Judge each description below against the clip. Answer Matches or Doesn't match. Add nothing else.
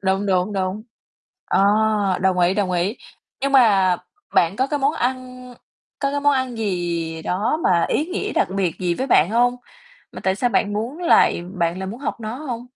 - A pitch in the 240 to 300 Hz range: Doesn't match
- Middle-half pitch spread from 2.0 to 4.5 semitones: Doesn't match